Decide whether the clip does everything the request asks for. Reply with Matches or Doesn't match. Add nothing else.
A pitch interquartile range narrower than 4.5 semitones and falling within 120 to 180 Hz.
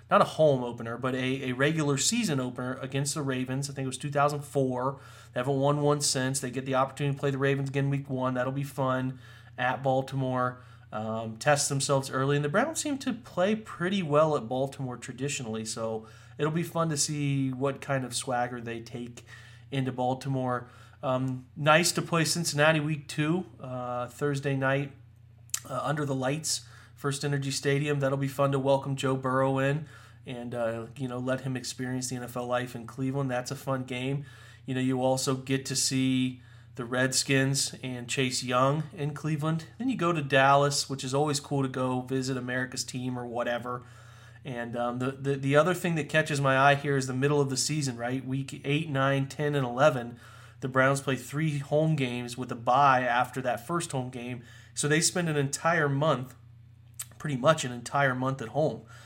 Matches